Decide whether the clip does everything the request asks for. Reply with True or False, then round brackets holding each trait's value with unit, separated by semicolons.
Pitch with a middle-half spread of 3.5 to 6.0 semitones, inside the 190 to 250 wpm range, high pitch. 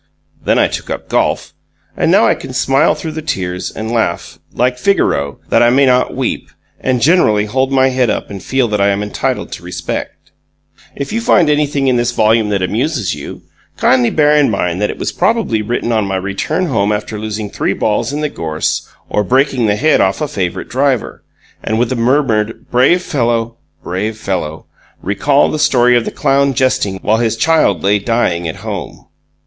False (4.8 semitones; 195 wpm; 115 Hz)